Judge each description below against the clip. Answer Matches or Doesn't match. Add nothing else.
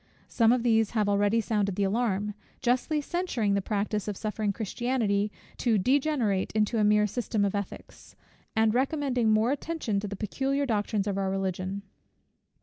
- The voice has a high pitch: Matches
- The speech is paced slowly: Doesn't match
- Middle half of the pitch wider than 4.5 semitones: Doesn't match